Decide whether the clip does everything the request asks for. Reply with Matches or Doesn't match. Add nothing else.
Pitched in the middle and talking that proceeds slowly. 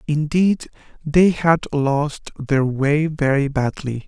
Matches